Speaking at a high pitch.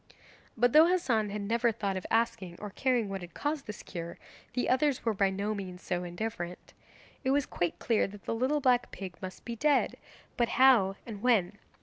Yes: high, 220 Hz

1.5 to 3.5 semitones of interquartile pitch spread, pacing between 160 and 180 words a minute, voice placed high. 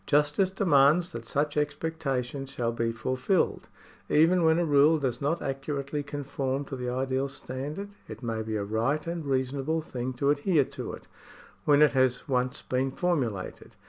No: average, 2.9 semitones; average, 165 wpm; medium, 140 Hz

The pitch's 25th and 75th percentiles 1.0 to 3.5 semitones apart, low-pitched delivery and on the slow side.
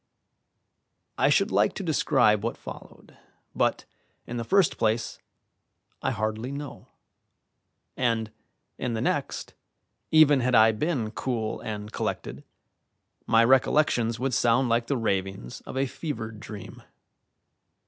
Yes: average, 3.2 semitones; low, 115 Hz; slow, 125 wpm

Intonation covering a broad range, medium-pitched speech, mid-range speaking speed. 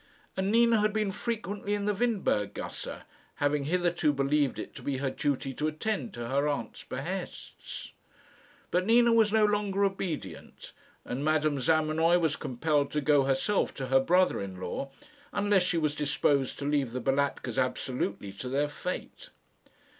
Yes: wide, 6.3 semitones; medium, 155 Hz; average, 160 wpm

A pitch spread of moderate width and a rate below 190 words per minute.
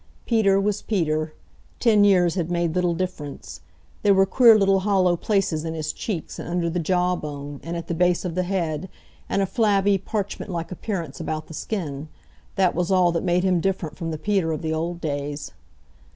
No: average, 3.2 semitones; average, 195 wpm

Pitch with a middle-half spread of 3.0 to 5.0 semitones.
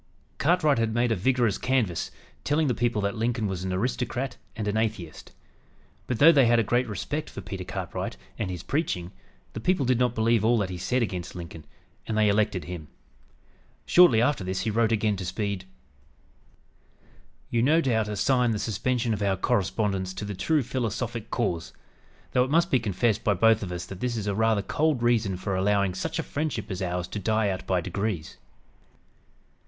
Yes: average, 4.2 semitones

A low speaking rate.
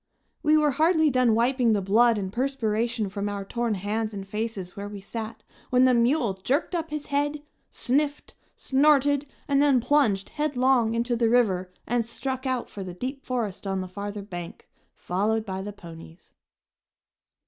No: average, 170 wpm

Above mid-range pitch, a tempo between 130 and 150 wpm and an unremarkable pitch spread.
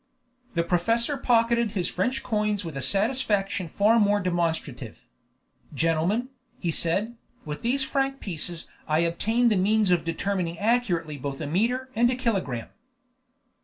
No: high, 200 Hz; average, 140 wpm; wide, 5.8 semitones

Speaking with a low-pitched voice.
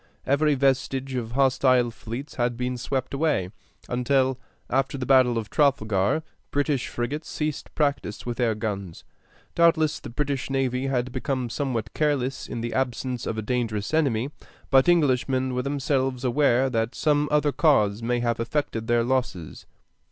Yes: low, 130 Hz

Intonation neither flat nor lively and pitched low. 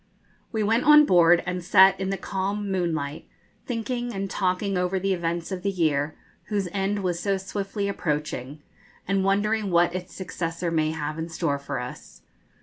No: average, 3.1 semitones; medium, 185 Hz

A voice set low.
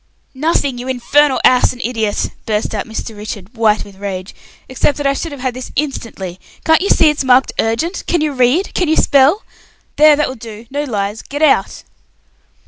No: very high, 255 Hz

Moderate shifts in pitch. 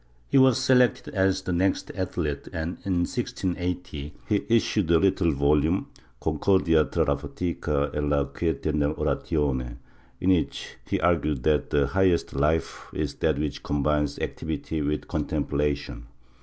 Yes: average, 4.2 semitones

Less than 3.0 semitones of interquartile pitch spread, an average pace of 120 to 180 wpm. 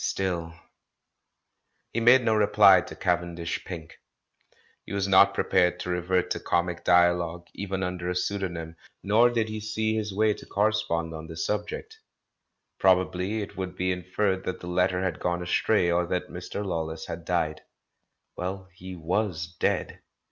Yes: narrow, 2.6 semitones; average, 155 wpm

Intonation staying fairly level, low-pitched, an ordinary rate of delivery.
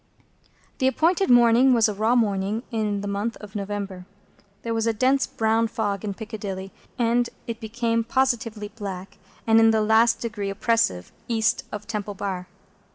No: narrow, 2.3 semitones; high, 220 Hz; average, 160 wpm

